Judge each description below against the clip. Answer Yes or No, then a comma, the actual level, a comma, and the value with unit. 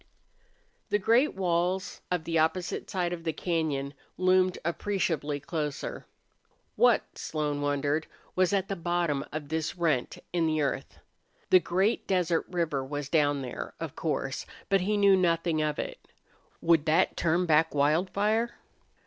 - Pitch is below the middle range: No, medium, 165 Hz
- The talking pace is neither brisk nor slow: Yes, average, 145 wpm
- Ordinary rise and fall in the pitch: Yes, average, 3.4 semitones